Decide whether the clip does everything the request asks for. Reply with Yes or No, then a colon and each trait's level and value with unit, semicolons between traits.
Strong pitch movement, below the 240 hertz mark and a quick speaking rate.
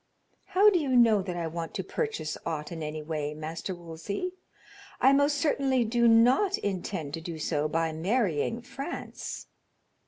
No: wide, 8.3 semitones; medium, 185 Hz; average, 160 wpm